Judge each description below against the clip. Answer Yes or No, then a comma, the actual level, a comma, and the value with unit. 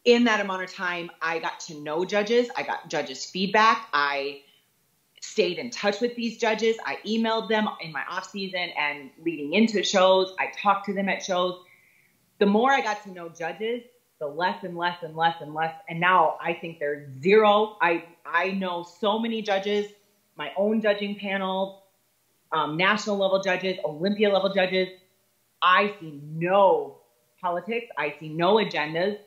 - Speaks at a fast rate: No, average, 170 wpm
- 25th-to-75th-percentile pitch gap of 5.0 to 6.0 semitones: No, average, 3.5 semitones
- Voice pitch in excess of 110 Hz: Yes, high, 190 Hz